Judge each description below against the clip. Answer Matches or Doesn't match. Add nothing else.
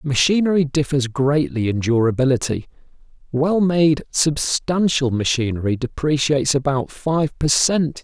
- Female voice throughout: Doesn't match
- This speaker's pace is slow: Matches